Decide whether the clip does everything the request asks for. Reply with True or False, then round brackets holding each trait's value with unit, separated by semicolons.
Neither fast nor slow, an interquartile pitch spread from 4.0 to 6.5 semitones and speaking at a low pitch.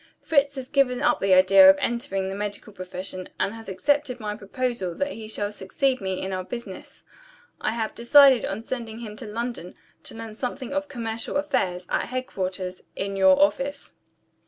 False (180 wpm; 4.8 semitones; 220 Hz)